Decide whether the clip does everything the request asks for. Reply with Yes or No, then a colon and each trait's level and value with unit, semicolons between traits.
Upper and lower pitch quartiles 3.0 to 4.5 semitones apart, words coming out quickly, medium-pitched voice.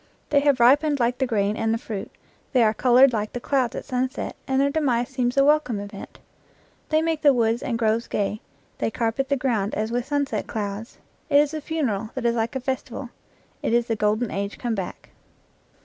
No: average, 3.6 semitones; fast, 210 wpm; high, 245 Hz